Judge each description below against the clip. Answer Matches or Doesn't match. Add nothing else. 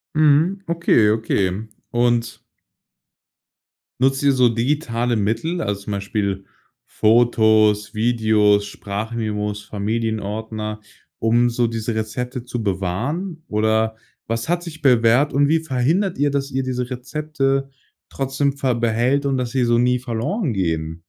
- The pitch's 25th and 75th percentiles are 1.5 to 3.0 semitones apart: Doesn't match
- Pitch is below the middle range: Matches